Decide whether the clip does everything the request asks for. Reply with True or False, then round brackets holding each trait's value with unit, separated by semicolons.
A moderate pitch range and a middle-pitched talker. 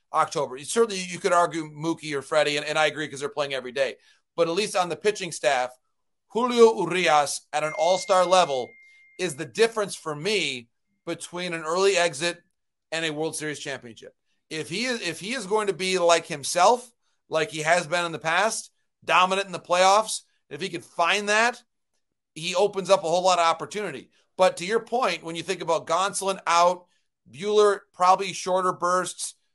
True (3.7 semitones; 175 Hz)